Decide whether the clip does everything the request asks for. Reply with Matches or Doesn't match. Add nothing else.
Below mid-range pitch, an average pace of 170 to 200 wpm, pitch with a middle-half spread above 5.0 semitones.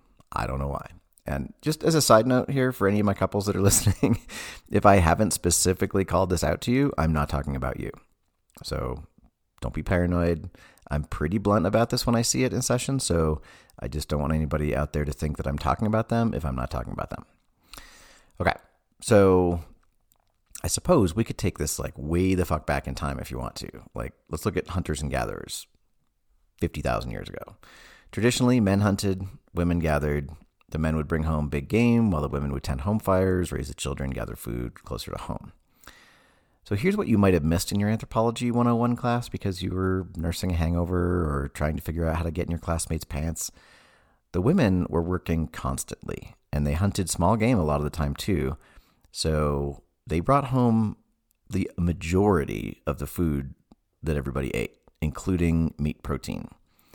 Matches